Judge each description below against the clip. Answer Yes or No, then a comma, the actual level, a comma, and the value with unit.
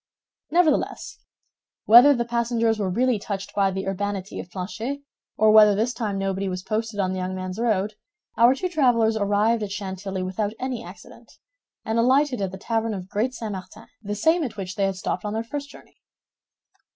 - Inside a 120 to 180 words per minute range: No, average, 190 wpm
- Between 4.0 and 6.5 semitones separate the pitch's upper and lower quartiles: No, average, 3.4 semitones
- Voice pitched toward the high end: Yes, high, 215 Hz